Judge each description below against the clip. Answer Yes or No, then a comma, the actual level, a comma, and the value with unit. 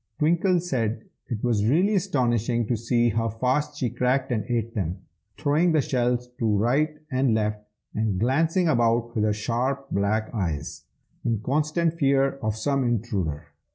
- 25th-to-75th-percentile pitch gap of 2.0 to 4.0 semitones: No, average, 4.4 semitones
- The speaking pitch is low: Yes, low, 120 Hz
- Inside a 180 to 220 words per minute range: No, average, 155 wpm